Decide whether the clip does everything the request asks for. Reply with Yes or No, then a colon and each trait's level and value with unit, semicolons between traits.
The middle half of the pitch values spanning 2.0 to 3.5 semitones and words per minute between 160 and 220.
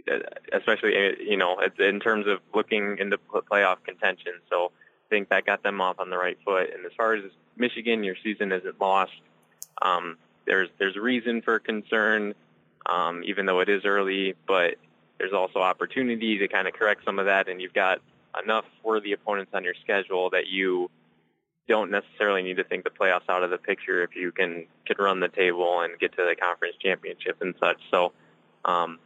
Yes: average, 3.2 semitones; average, 190 wpm